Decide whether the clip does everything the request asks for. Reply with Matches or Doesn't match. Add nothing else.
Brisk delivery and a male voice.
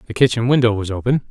Matches